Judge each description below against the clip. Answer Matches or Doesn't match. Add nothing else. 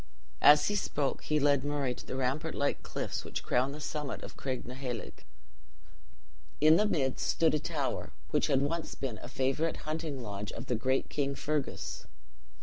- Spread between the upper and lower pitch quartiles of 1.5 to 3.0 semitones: Matches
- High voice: Doesn't match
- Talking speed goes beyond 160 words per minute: Matches